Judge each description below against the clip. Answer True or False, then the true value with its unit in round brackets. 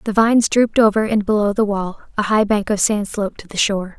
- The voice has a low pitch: False (210 Hz)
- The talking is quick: True (255 wpm)